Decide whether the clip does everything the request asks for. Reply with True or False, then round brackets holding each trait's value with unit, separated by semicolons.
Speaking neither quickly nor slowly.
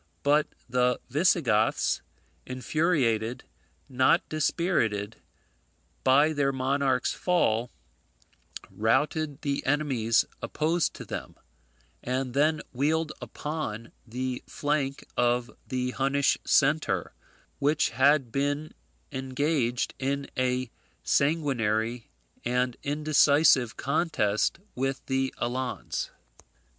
False (85 wpm)